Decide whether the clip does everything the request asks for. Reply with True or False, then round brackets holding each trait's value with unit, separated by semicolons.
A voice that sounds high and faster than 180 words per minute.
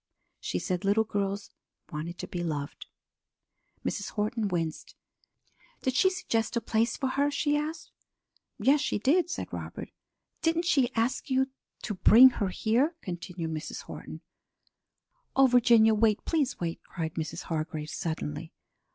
False (220 Hz; 140 wpm)